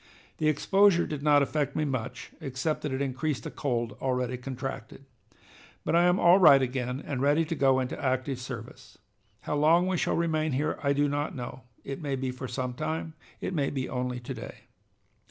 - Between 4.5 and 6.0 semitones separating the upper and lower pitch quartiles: No, average, 3.2 semitones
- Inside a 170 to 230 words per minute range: Yes, average, 195 wpm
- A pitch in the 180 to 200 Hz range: No, medium, 140 Hz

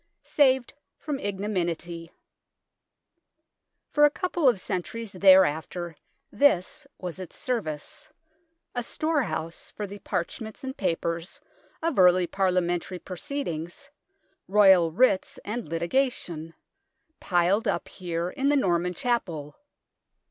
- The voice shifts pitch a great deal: Yes, wide, 6.4 semitones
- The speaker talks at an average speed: No, slow, 105 wpm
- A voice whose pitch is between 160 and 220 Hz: Yes, high, 190 Hz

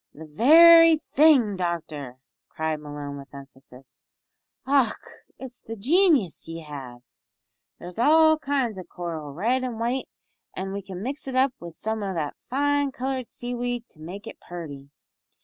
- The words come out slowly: No, average, 150 wpm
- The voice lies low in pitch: No, high, 210 Hz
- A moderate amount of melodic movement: No, wide, 8.9 semitones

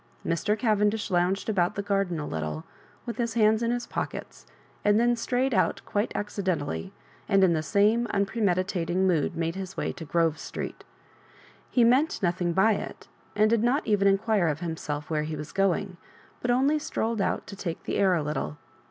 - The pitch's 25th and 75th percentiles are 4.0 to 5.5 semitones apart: Yes, average, 4.6 semitones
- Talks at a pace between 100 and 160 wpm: No, average, 190 wpm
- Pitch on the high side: Yes, high, 195 Hz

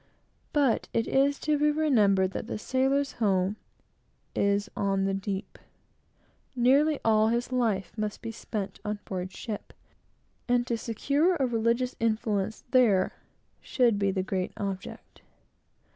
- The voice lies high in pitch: Yes, high, 225 Hz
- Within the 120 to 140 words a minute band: Yes, slow, 135 wpm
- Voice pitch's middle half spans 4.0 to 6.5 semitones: Yes, average, 4.4 semitones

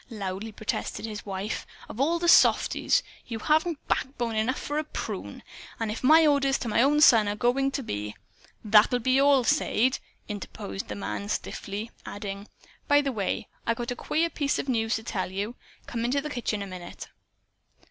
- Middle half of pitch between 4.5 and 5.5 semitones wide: Yes, average, 4.9 semitones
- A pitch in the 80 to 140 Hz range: No, high, 230 Hz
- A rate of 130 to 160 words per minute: No, average, 190 wpm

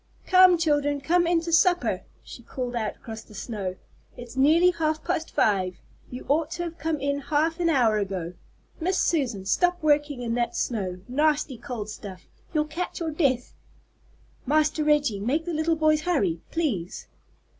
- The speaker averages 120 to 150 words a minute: No, average, 165 wpm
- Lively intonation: Yes, wide, 5.9 semitones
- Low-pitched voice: No, very high, 290 Hz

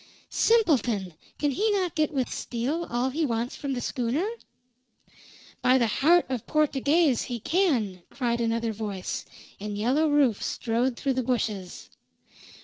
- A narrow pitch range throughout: No, average, 4.8 semitones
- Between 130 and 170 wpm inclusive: Yes, average, 140 wpm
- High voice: Yes, very high, 255 Hz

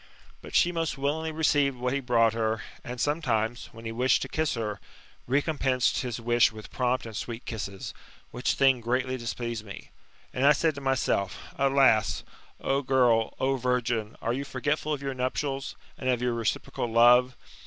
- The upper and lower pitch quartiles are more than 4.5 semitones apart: No, average, 2.9 semitones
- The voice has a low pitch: Yes, low, 125 Hz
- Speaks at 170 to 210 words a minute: Yes, average, 175 wpm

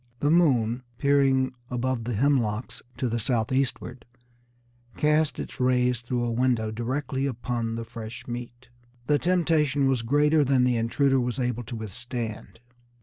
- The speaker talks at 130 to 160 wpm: Yes, average, 145 wpm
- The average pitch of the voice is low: Yes, low, 125 Hz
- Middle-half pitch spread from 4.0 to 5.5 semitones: No, average, 2.8 semitones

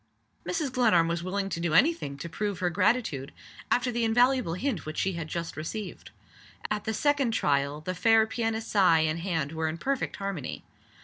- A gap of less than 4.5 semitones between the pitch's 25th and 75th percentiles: No, wide, 5.5 semitones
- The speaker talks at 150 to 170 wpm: No, average, 190 wpm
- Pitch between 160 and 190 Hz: Yes, medium, 185 Hz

